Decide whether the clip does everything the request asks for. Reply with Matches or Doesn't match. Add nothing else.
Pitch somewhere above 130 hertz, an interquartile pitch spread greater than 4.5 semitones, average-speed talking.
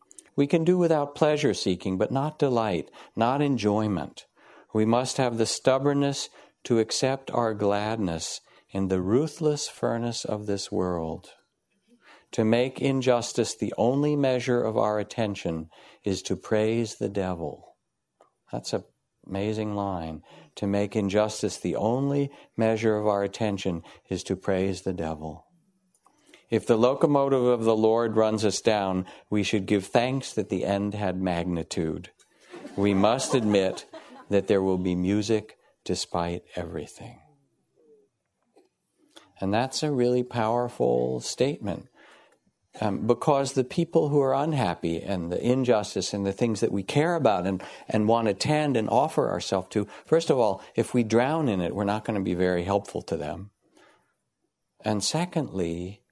Doesn't match